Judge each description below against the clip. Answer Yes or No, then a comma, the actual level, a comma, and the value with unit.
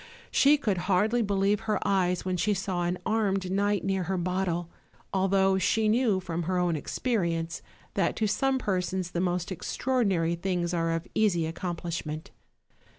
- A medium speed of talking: Yes, average, 160 wpm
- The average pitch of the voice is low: No, medium, 185 Hz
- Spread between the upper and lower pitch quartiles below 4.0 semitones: Yes, average, 2.9 semitones